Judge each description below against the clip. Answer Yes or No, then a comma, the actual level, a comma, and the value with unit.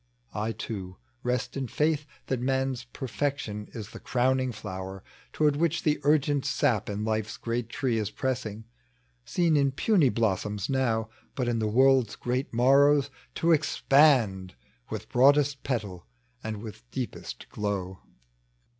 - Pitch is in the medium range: No, low, 125 Hz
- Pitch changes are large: No, average, 4.7 semitones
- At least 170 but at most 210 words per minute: No, average, 140 wpm